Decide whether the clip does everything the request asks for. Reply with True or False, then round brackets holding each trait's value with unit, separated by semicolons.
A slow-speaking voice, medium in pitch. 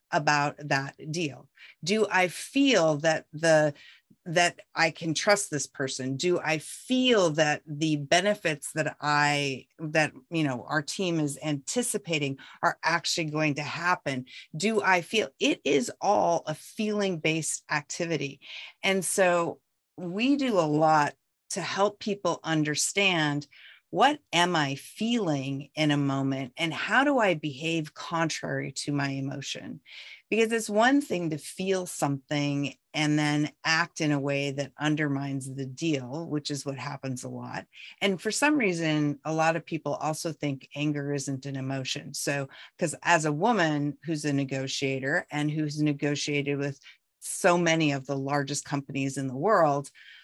False (155 wpm; 150 Hz)